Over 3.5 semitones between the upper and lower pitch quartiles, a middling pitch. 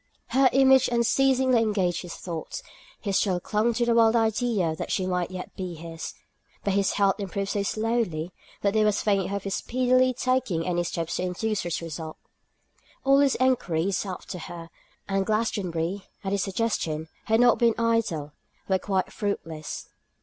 No: average, 4.6 semitones; high, 200 Hz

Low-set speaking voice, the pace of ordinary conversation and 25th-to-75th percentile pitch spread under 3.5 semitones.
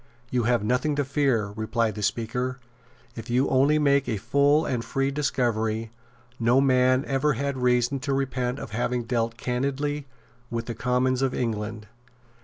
Yes: low, 125 Hz; average, 165 wpm; average, 2.9 semitones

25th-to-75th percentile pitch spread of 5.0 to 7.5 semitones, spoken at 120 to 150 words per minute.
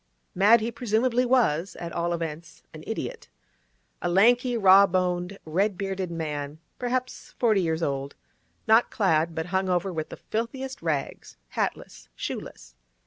Yes: wide, 5.4 semitones; average, 140 wpm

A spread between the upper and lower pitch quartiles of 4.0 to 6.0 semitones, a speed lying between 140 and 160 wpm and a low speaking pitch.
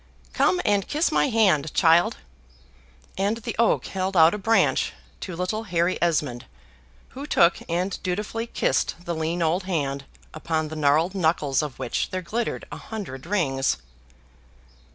No: average, 4.4 semitones; average, 150 wpm; medium, 175 Hz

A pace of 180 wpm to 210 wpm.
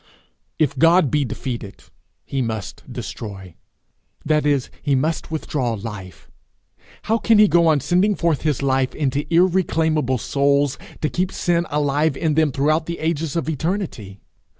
No: average, 150 wpm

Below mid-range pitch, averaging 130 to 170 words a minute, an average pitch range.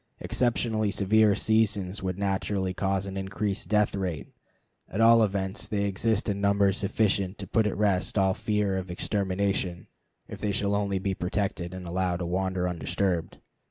No: low, 100 Hz; average, 160 wpm; narrow, 1.8 semitones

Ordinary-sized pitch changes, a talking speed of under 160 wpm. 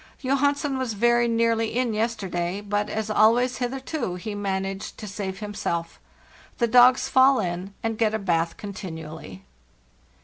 Yes: average, 3.9 semitones; average, 145 wpm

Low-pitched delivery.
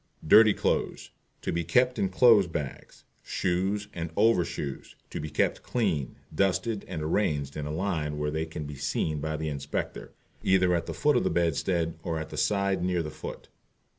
Yes: very low, 85 Hz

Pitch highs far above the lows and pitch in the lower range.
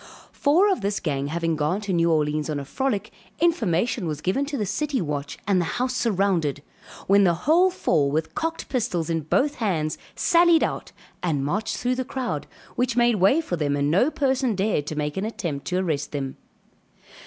No: wide, 8.5 semitones; high, 190 Hz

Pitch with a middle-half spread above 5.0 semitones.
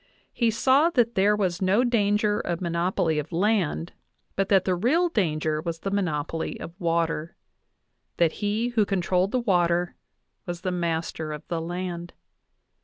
No: average, 3.7 semitones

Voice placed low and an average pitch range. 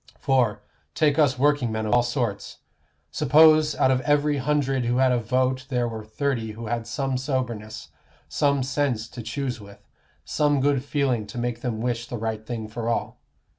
Yes: low, 125 Hz; average, 3.5 semitones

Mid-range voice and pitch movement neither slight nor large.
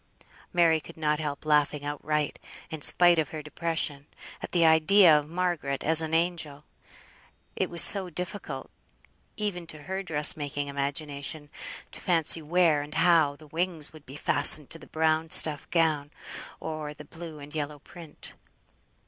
No: medium, 155 Hz; narrow, 2.3 semitones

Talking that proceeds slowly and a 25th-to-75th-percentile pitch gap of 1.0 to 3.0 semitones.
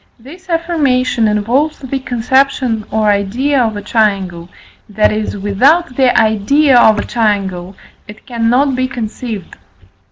No: slow, 130 wpm; average, 4.3 semitones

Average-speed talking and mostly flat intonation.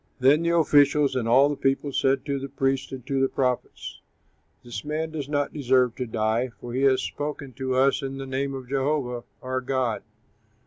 Yes: average, 195 wpm; narrow, 1.7 semitones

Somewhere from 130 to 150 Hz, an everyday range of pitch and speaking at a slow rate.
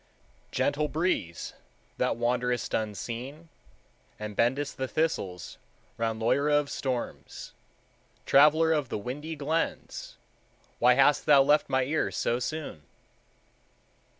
Yes: low, 135 Hz; average, 4.1 semitones; slow, 110 wpm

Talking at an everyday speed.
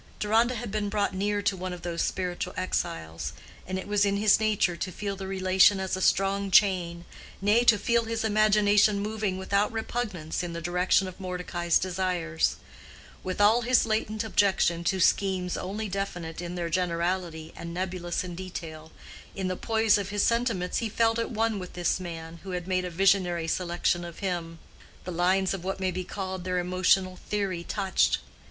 Yes: average, 180 wpm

